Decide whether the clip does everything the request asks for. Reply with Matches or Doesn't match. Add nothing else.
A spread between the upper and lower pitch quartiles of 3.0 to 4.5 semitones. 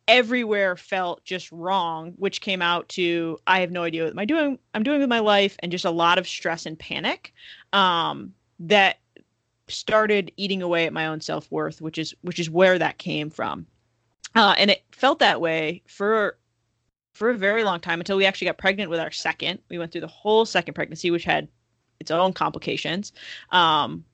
Matches